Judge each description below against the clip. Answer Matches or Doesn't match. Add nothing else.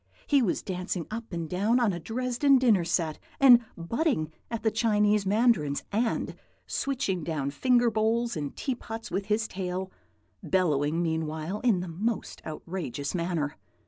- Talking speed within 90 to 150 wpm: Matches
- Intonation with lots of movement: Matches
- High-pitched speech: Matches